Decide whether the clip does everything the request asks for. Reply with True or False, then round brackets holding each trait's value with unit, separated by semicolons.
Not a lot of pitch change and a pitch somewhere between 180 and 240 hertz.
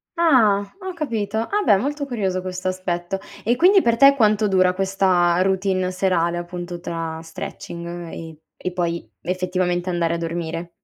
False (3.3 semitones; 185 Hz)